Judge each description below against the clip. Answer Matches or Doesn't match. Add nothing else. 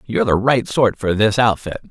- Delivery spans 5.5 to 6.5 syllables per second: Doesn't match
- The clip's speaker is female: Doesn't match